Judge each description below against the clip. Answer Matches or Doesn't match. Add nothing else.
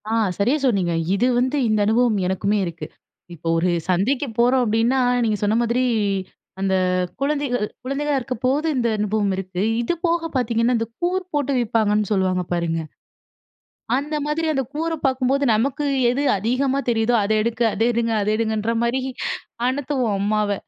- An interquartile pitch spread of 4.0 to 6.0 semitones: Matches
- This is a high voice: Matches